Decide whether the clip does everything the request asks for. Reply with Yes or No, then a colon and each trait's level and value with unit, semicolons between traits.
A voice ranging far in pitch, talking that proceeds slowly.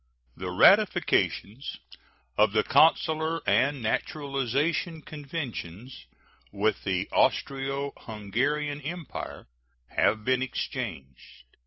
Yes: wide, 5.8 semitones; slow, 80 wpm